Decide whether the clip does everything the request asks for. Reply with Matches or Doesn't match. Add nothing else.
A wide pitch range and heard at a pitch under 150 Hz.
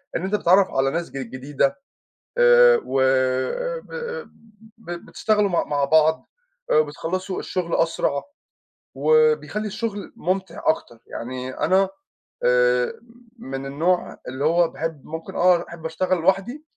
Doesn't match